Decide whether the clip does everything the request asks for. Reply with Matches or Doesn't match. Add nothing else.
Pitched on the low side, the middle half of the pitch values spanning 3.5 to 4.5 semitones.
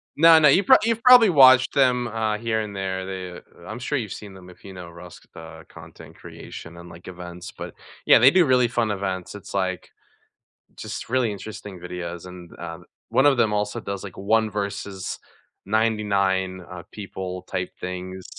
Matches